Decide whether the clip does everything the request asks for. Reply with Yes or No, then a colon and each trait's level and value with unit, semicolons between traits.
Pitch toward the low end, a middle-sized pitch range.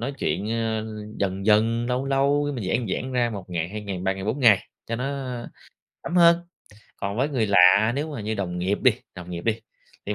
Yes: low, 110 Hz; average, 4.4 semitones